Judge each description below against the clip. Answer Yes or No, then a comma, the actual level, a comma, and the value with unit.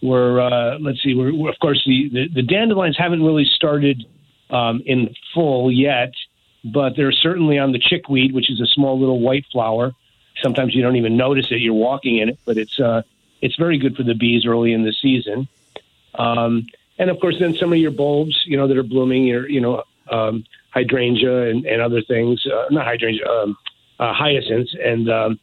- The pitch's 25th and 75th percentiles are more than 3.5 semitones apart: No, average, 3.1 semitones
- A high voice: No, low, 130 Hz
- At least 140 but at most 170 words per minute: No, fast, 205 wpm